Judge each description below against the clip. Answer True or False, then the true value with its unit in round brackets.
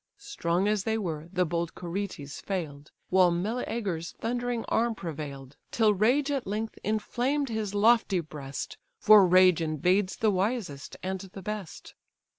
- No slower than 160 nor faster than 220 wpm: False (140 wpm)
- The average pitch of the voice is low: False (190 Hz)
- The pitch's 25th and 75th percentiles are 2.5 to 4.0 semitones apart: False (4.6 semitones)